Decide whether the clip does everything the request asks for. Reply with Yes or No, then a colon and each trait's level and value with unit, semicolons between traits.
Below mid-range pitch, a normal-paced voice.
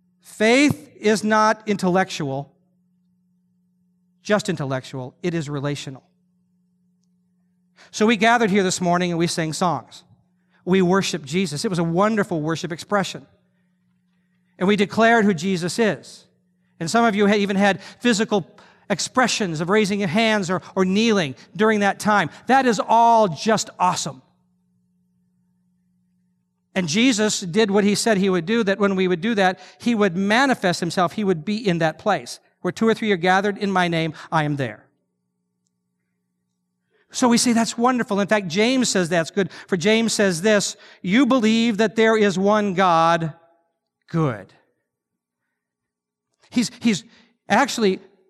No: medium, 185 Hz; average, 150 wpm